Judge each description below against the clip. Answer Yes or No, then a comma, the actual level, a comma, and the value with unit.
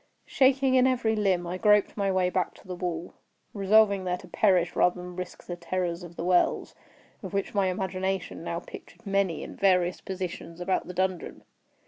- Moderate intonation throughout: No, narrow, 2.0 semitones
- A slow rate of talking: No, average, 180 wpm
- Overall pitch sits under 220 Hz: Yes, medium, 185 Hz